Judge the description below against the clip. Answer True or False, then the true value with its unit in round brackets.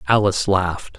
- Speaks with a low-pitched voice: True (95 Hz)